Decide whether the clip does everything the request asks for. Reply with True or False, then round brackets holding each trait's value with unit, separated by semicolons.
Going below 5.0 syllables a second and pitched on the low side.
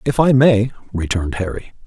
False (5.6 syllables/s; 110 Hz)